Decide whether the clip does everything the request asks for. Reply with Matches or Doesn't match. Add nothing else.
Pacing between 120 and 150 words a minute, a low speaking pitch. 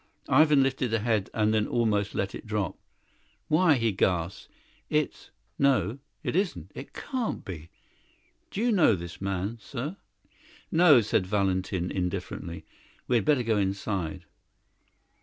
Matches